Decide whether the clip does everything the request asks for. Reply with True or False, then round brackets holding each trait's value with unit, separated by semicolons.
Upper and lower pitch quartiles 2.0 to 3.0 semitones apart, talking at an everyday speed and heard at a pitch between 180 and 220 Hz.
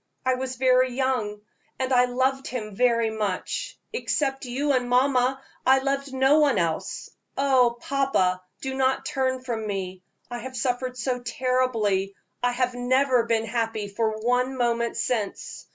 False (2.5 semitones; 150 wpm; 250 Hz)